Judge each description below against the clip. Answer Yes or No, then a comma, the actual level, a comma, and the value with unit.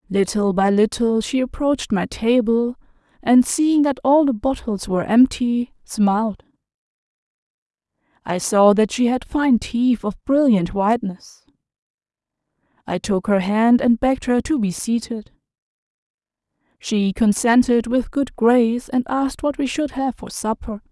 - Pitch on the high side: Yes, high, 235 Hz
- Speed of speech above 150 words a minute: No, average, 140 wpm